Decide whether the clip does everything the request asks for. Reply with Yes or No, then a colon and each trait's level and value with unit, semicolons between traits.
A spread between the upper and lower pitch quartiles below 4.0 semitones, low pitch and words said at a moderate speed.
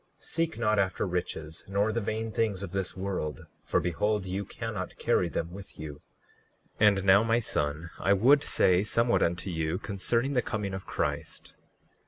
Yes: average, 3.5 semitones; low, 100 Hz; average, 180 wpm